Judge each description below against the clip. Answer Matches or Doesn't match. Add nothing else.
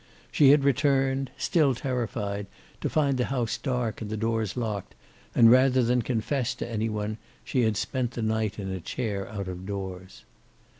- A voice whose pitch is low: Matches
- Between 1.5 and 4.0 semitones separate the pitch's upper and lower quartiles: Matches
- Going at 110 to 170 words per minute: Doesn't match